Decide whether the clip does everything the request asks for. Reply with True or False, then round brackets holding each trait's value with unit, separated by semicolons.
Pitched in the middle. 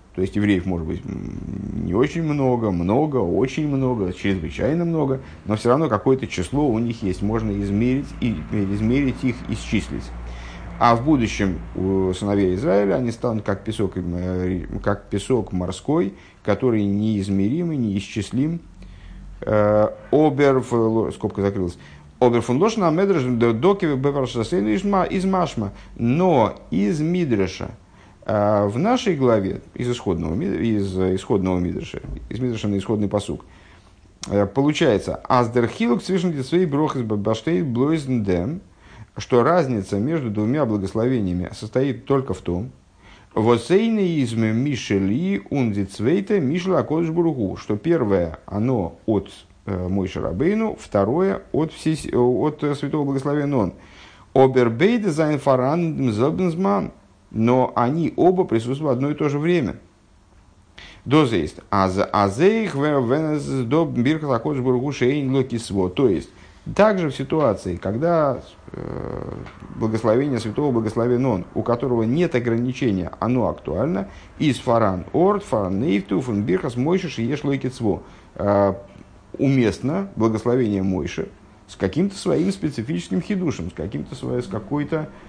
False (120 Hz)